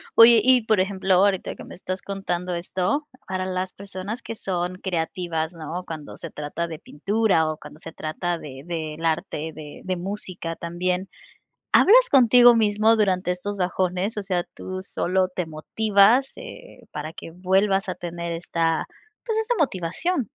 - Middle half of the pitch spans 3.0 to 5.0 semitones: Yes, average, 3.4 semitones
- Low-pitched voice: No, medium, 185 Hz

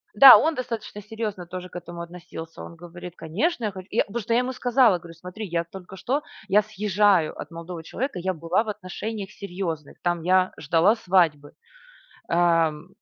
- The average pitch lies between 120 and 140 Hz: No, medium, 185 Hz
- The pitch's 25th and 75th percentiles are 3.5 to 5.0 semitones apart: Yes, average, 4.0 semitones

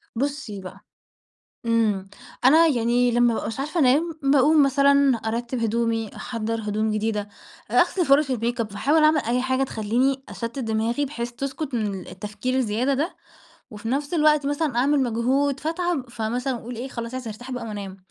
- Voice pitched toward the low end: No, high, 245 Hz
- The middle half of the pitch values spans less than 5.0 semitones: Yes, average, 3.7 semitones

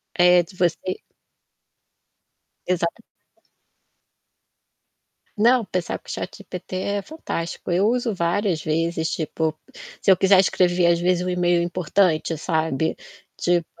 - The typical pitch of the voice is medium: Yes, medium, 175 Hz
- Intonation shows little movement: Yes, narrow, 2.1 semitones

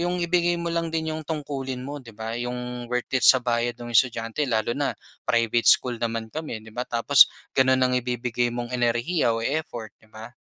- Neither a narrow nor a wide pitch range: Yes, average, 3.6 semitones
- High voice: No, low, 125 Hz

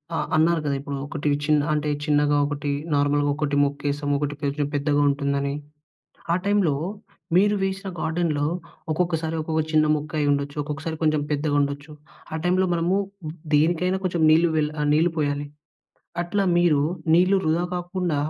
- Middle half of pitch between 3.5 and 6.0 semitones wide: No, average, 2.9 semitones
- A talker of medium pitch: Yes, medium, 150 Hz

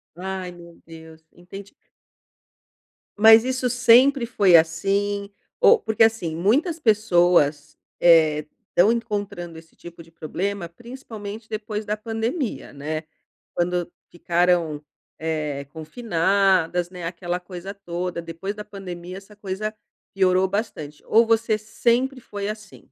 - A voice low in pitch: No, high, 190 Hz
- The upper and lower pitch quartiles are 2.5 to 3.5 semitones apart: No, average, 4.2 semitones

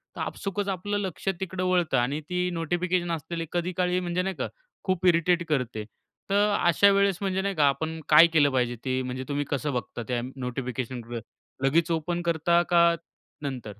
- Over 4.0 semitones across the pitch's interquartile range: Yes, average, 5.1 semitones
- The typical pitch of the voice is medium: Yes, medium, 170 Hz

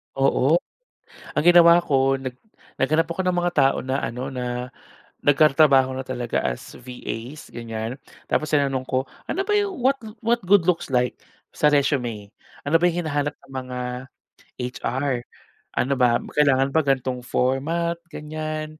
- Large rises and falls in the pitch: No, average, 3.7 semitones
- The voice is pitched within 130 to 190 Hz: Yes, low, 135 Hz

